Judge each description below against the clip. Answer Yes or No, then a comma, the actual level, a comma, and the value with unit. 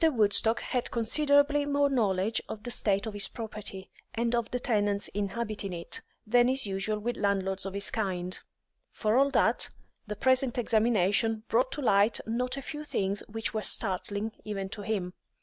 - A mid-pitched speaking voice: No, high, 220 Hz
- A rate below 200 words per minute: Yes, average, 170 wpm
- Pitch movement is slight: No, average, 3.3 semitones